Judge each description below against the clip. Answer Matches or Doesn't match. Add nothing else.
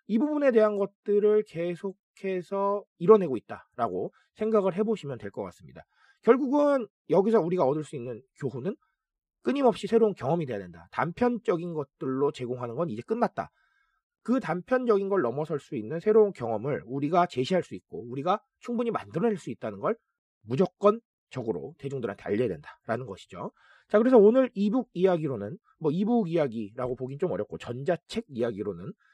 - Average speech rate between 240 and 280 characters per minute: Doesn't match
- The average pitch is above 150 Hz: Matches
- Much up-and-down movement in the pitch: Matches